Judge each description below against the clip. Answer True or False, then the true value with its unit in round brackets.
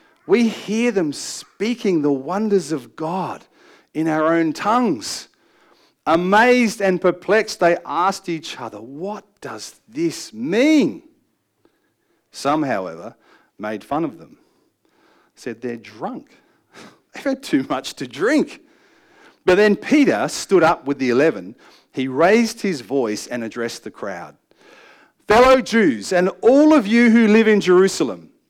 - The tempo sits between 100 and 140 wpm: True (135 wpm)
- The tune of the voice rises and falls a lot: True (8.6 semitones)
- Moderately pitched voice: False (210 Hz)